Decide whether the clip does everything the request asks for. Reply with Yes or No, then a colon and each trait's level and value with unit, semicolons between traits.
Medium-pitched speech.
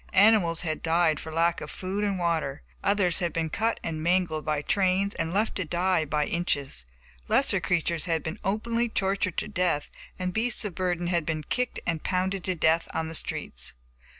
Yes: medium, 175 Hz